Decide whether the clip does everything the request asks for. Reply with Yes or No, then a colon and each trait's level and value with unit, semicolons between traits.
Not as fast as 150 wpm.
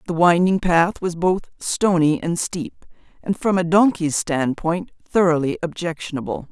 Yes: average, 140 wpm